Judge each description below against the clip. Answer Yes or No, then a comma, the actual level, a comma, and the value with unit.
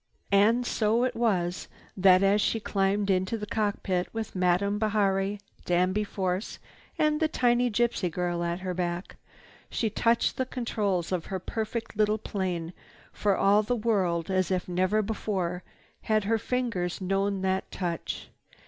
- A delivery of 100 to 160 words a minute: Yes, average, 150 wpm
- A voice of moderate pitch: No, high, 200 Hz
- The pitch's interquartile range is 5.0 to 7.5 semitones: No, average, 3.1 semitones